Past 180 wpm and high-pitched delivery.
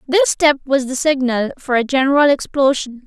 No: average, 175 wpm; very high, 270 Hz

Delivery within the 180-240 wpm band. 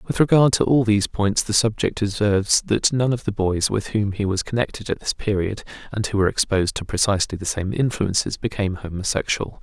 Yes: fast, 205 wpm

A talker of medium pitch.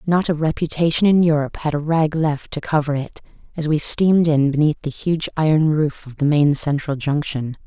Yes: medium, 150 Hz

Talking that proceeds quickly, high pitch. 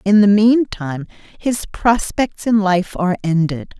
No: average, 140 wpm; high, 200 Hz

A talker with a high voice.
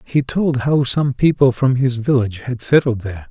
No: low, 130 Hz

